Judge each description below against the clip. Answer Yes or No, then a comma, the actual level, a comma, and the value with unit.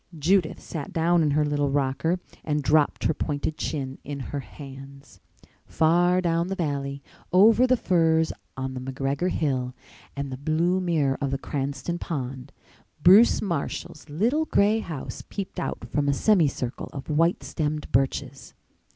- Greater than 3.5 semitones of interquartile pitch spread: Yes, average, 4.0 semitones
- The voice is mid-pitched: Yes, medium, 150 Hz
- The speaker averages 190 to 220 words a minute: No, average, 150 wpm